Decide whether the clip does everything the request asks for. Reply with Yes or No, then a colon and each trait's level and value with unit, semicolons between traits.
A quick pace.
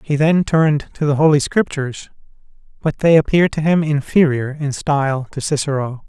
No: average, 170 wpm